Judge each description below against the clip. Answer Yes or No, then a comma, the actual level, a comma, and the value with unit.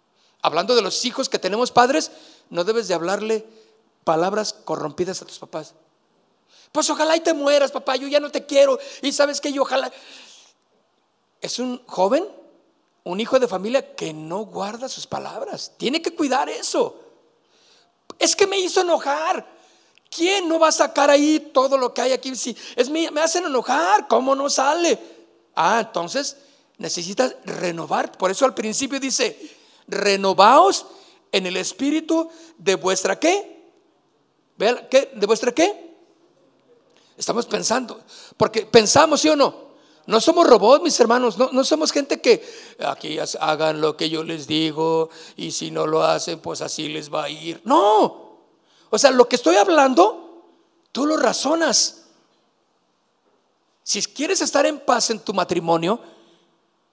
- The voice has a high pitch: Yes, very high, 265 Hz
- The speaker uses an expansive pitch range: Yes, wide, 7.8 semitones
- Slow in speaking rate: No, average, 150 wpm